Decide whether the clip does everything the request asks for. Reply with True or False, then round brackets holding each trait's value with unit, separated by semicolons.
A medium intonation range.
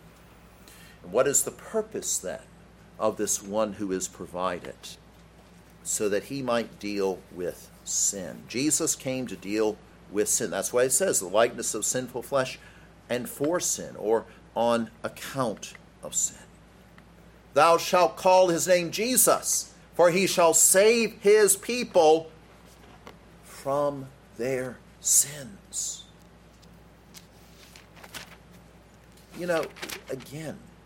False (8.9 semitones)